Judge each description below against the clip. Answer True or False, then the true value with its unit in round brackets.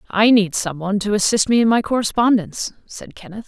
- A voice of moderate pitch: False (210 Hz)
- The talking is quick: False (190 wpm)